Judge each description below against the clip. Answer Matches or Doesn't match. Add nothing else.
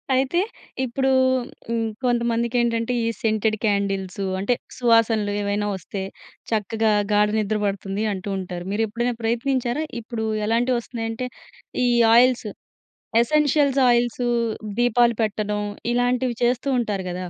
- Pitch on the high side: Matches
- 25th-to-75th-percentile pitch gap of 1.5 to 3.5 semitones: Matches